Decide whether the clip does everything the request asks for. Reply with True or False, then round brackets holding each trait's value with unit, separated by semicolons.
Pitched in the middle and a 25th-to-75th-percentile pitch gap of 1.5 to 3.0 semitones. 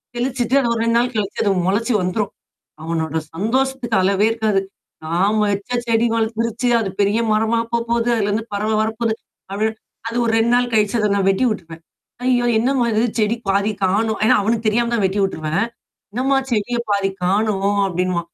False (220 Hz; 2.7 semitones)